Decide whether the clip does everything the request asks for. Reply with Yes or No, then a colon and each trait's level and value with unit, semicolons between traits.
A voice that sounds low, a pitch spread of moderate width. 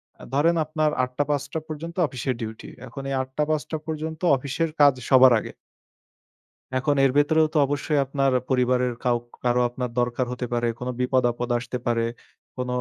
Yes: low, 130 Hz; average, 3.2 semitones